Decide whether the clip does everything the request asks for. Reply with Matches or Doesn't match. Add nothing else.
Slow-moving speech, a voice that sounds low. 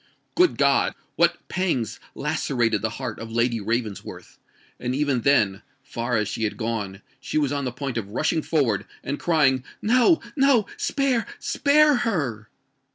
Matches